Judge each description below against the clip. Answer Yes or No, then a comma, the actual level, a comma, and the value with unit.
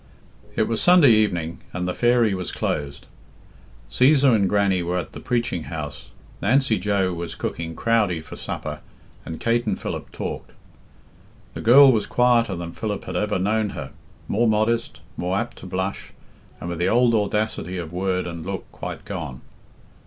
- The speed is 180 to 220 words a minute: No, average, 165 wpm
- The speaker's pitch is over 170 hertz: No, low, 100 Hz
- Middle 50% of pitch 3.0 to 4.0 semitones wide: No, average, 4.7 semitones